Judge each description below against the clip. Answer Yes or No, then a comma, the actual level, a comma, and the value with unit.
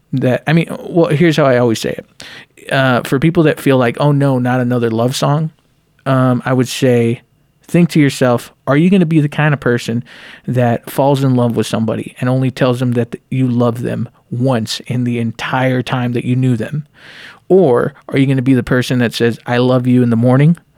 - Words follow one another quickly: Yes, fast, 225 wpm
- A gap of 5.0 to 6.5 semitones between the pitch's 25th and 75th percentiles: No, average, 3.0 semitones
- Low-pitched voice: Yes, low, 130 Hz